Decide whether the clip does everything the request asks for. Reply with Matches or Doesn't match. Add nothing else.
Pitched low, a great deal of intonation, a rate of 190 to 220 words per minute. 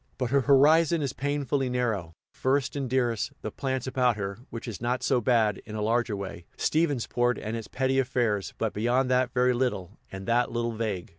Doesn't match